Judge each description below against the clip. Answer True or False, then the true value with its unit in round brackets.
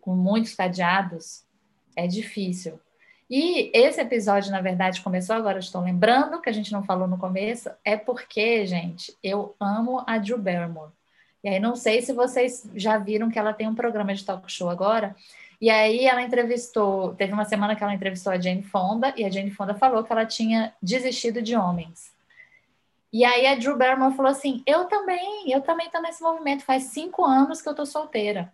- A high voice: True (220 Hz)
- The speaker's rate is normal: False (190 wpm)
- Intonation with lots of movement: False (4.8 semitones)